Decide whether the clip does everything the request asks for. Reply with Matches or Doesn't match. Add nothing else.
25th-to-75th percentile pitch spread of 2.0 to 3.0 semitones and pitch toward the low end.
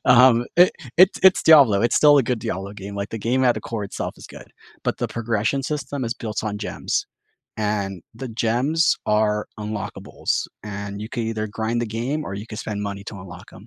Doesn't match